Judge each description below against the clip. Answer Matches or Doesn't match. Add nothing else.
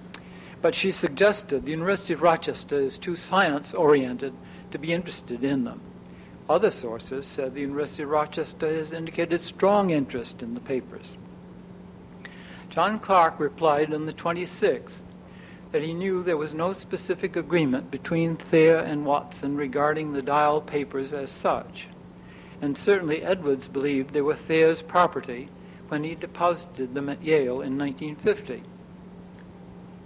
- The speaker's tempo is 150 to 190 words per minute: Doesn't match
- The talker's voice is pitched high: Doesn't match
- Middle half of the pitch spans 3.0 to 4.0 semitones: Matches